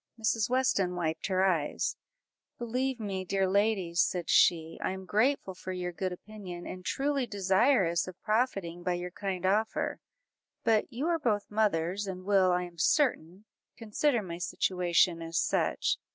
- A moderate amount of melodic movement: Yes, average, 3.6 semitones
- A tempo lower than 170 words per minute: Yes, average, 155 wpm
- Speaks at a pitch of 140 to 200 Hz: Yes, high, 190 Hz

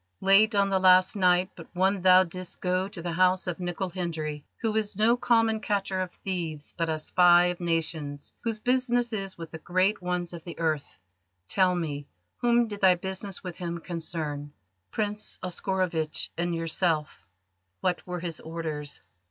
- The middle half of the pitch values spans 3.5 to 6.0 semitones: No, average, 2.8 semitones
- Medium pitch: Yes, medium, 180 Hz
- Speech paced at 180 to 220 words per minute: No, average, 170 wpm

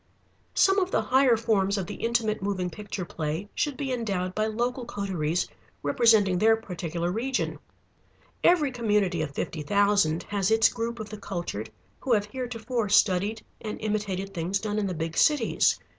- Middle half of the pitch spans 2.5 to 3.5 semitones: No, average, 4.0 semitones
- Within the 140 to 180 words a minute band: Yes, average, 165 wpm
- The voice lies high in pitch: Yes, high, 210 Hz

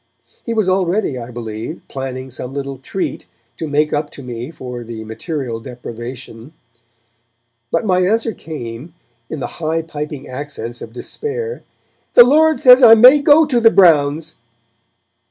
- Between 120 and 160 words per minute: Yes, average, 150 wpm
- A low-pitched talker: No, medium, 150 Hz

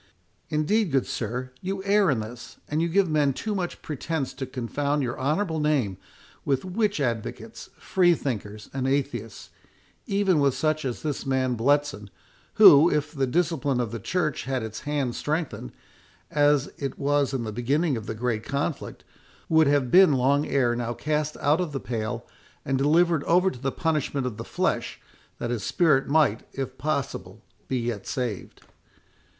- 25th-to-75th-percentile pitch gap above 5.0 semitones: No, average, 4.0 semitones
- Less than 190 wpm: Yes, average, 165 wpm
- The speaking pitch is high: No, medium, 140 Hz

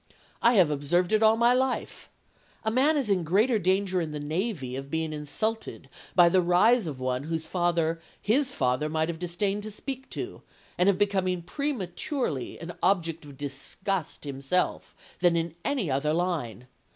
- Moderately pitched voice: Yes, medium, 175 Hz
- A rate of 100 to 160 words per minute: No, average, 170 wpm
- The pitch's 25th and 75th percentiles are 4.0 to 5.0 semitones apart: No, wide, 5.4 semitones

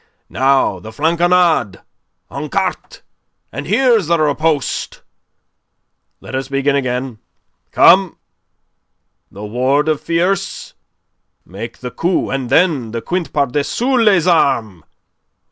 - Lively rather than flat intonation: Yes, wide, 5.9 semitones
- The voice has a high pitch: No, medium, 145 Hz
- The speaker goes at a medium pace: No, slow, 115 wpm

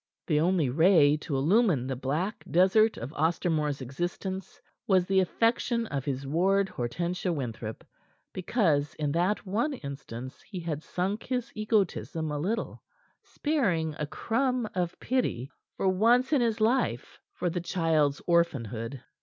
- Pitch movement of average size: No, wide, 6.4 semitones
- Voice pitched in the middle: Yes, medium, 175 Hz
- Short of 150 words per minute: Yes, average, 140 wpm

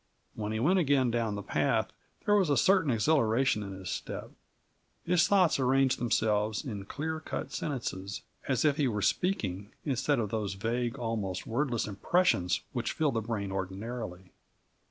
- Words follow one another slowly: No, average, 160 wpm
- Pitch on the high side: No, low, 115 Hz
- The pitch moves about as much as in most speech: No, wide, 5.7 semitones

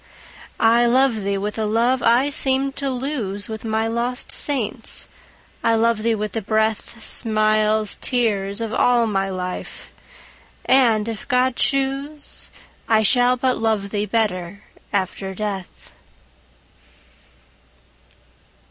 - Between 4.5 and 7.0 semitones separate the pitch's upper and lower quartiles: No, average, 3.0 semitones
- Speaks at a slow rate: Yes, slow, 115 wpm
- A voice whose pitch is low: No, high, 225 Hz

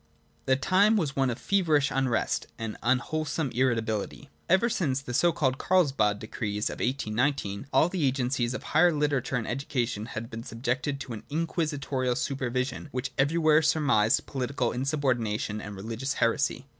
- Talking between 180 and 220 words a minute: No, average, 160 wpm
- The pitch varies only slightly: No, average, 4.0 semitones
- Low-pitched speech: Yes, low, 130 Hz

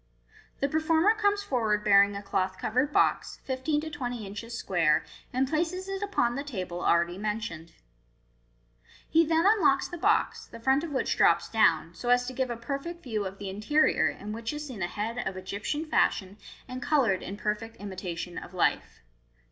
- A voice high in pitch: Yes, high, 235 Hz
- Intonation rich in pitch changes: Yes, wide, 7.0 semitones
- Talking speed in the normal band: Yes, average, 180 wpm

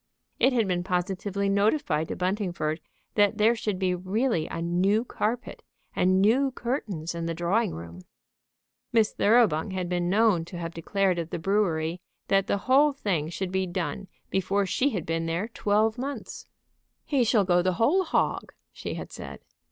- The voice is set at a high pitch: Yes, high, 195 Hz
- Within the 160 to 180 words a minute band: Yes, average, 170 wpm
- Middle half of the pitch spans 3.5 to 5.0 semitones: Yes, average, 4.1 semitones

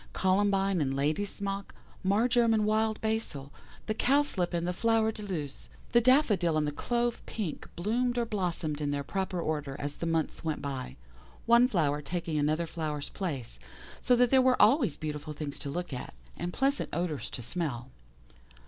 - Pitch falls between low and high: Yes, medium, 180 Hz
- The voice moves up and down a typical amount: No, wide, 6.8 semitones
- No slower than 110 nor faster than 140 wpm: No, average, 170 wpm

